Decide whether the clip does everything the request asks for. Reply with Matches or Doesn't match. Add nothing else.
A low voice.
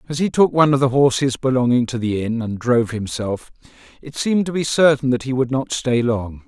Matches